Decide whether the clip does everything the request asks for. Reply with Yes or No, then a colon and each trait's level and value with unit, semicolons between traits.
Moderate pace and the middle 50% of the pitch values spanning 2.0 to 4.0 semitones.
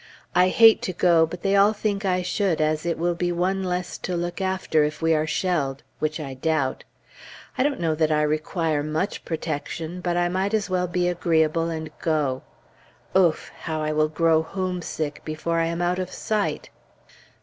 Yes: average, 190 wpm; average, 2.8 semitones